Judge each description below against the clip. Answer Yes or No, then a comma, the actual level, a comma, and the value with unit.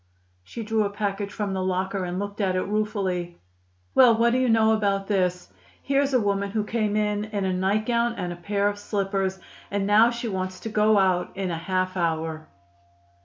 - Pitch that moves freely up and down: No, narrow, 2.5 semitones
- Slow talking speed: No, average, 195 wpm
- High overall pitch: Yes, high, 200 Hz